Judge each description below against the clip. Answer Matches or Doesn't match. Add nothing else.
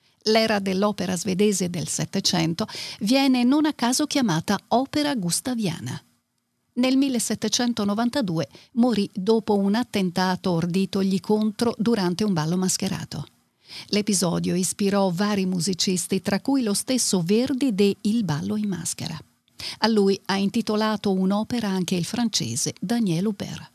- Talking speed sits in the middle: Matches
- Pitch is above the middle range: Matches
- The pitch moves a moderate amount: Matches